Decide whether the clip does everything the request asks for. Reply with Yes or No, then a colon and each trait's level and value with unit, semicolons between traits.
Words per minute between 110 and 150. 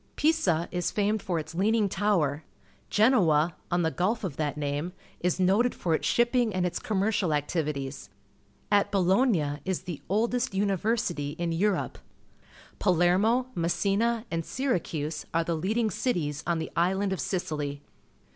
Yes: average, 145 wpm